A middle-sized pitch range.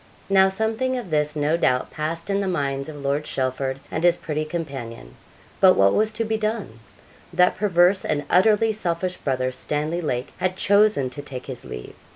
No: wide, 6.0 semitones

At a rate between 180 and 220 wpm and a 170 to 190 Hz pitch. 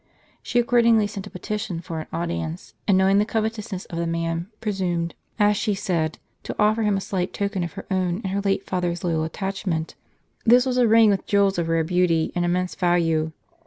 Yes: average, 200 wpm; medium, 185 Hz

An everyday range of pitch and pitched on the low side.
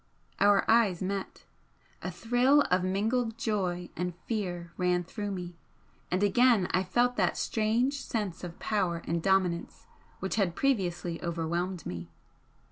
No: average, 3.9 semitones; high, 190 Hz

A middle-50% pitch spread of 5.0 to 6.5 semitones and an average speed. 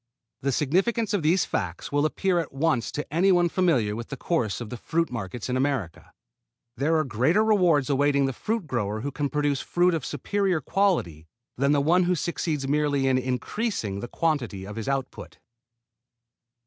Yes: wide, 5.5 semitones; average, 180 wpm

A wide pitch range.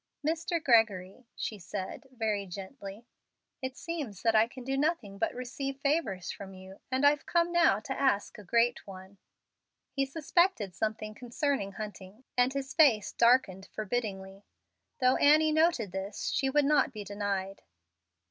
Yes: wide, 5.8 semitones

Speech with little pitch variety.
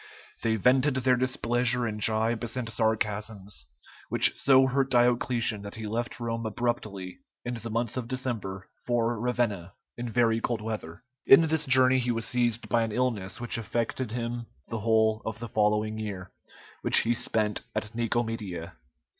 Yes: narrow, 2.2 semitones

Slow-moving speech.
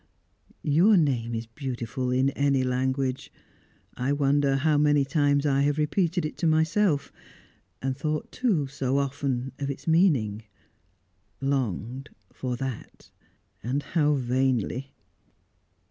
Yes: slow, 120 wpm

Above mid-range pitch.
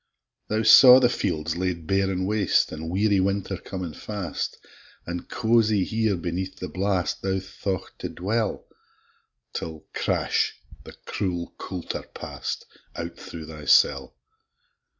No: very low, 95 Hz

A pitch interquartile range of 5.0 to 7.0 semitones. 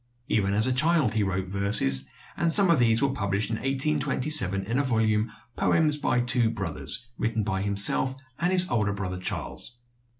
Yes: wide, 5.4 semitones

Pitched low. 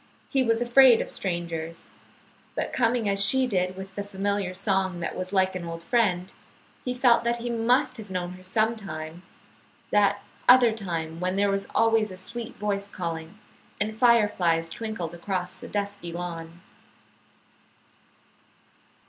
No: high, 200 Hz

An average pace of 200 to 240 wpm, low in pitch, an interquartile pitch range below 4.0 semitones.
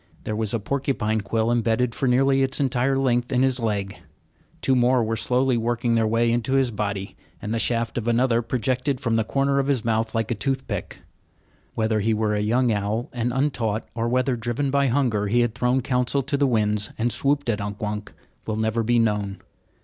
Yes: fast, 205 wpm; low, 120 Hz; average, 2.8 semitones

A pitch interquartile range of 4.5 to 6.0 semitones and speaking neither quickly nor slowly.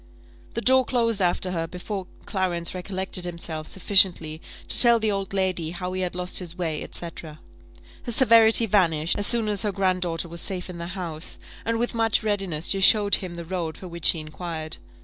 No: average, 3.2 semitones; average, 195 wpm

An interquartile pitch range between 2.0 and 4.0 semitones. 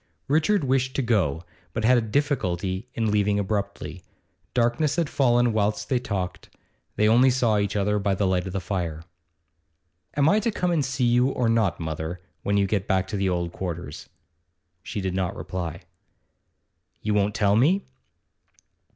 No: average, 4.9 semitones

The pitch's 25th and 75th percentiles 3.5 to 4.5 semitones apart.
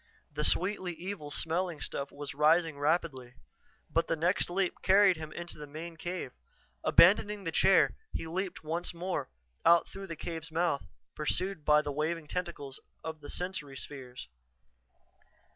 No: average, 3.0 semitones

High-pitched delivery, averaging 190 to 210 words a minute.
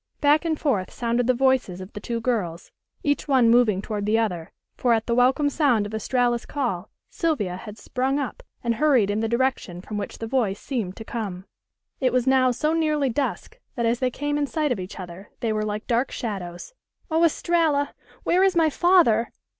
Yes: high, 240 Hz; average, 200 wpm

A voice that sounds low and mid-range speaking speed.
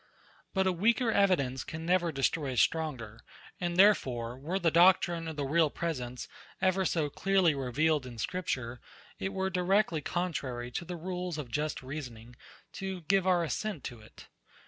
No: medium, 165 Hz; average, 165 wpm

